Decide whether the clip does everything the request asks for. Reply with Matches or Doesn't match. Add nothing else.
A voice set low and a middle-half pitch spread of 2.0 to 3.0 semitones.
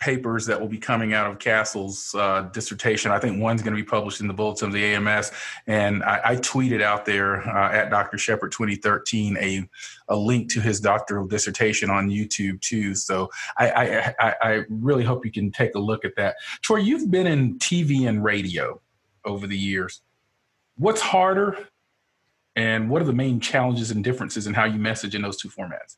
Matches